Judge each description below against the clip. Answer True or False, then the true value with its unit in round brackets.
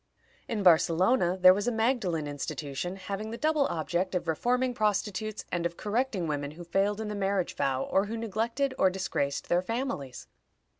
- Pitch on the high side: True (195 Hz)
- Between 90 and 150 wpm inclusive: False (170 wpm)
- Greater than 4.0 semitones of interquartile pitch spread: True (4.6 semitones)